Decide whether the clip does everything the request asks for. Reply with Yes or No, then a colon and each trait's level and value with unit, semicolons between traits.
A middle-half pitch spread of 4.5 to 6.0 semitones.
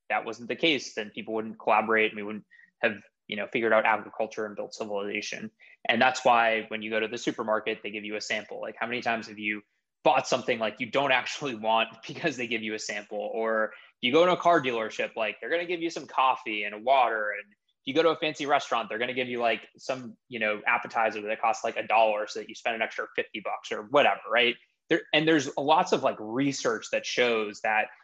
No: average, 3.9 semitones